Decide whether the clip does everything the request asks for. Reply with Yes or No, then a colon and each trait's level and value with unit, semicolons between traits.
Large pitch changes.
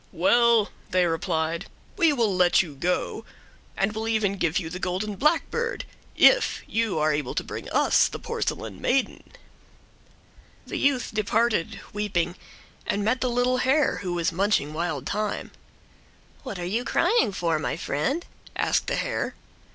Yes: wide, 5.8 semitones